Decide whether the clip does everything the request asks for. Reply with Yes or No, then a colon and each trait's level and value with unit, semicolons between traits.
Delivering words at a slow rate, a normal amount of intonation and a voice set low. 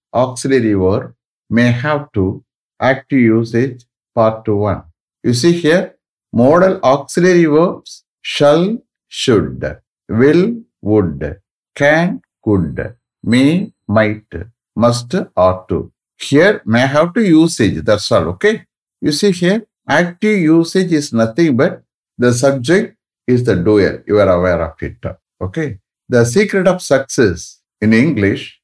No: slow, 125 wpm; wide, 7.3 semitones; low, 130 Hz